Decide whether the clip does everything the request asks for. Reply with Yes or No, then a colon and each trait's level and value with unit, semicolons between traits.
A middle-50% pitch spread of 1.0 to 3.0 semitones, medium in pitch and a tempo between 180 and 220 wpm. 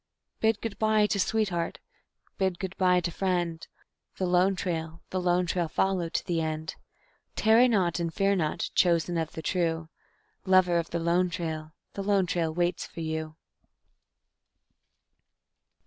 No: narrow, 2.5 semitones; medium, 175 Hz; average, 150 wpm